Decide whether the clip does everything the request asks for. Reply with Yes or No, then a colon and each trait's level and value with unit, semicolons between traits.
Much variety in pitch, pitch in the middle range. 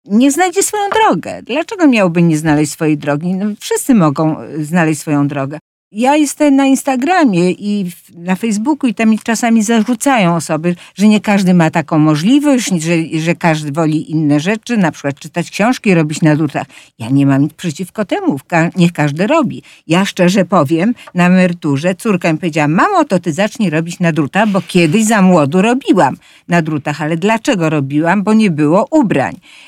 Yes: wide, 6.1 semitones; medium, 180 Hz